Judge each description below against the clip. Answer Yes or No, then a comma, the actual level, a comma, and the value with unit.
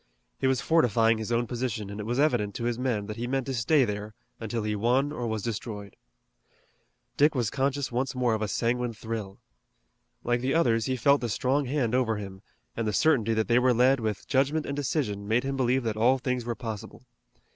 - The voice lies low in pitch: Yes, low, 120 Hz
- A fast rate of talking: Yes, fast, 215 wpm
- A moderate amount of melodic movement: Yes, average, 3.1 semitones